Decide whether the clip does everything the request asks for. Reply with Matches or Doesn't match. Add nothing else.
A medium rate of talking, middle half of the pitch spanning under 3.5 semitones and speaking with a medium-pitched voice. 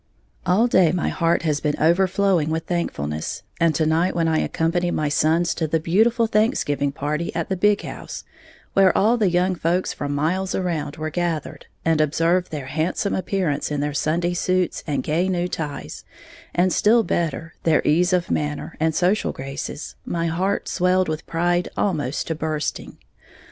Matches